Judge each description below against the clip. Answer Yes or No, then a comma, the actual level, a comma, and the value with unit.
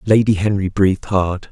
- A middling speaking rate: Yes, average, 160 wpm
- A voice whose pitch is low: Yes, low, 100 Hz